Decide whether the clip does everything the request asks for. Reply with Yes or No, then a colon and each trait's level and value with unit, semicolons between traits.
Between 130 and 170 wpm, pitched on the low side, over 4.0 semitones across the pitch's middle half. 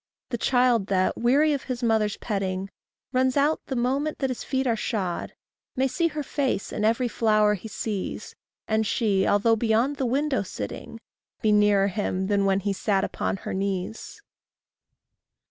No: average, 165 wpm; high, 220 Hz; average, 4.4 semitones